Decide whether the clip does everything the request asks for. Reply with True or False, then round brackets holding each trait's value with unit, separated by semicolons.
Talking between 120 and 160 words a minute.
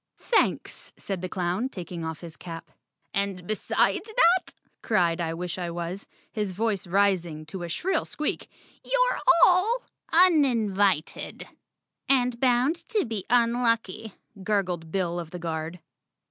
True (135 wpm)